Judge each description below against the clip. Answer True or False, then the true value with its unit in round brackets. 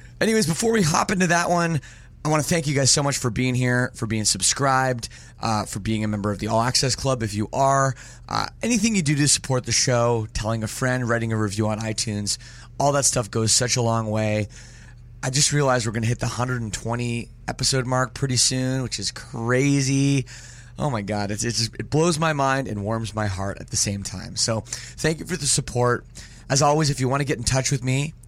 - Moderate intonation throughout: True (3.5 semitones)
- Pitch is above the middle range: False (125 Hz)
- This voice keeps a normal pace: False (230 wpm)